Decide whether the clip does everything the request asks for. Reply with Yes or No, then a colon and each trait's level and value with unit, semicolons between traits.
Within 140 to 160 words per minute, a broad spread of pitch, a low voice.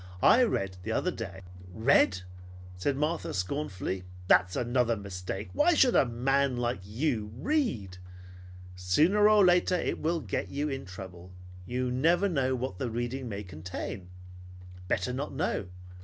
Yes: average, 150 wpm; wide, 7.9 semitones; low, 120 Hz